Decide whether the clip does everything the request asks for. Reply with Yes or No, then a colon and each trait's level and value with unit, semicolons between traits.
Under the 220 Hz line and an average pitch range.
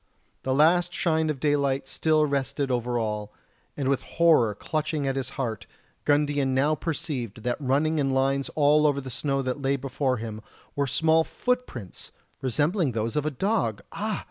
Yes: medium, 140 Hz; average, 3.1 semitones